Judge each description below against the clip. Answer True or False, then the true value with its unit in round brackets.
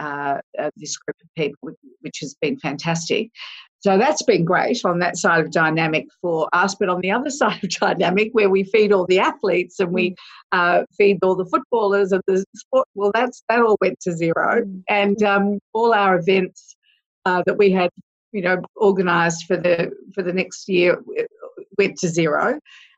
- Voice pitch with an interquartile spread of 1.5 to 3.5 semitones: True (2.7 semitones)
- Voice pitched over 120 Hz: True (190 Hz)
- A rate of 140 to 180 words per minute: False (190 wpm)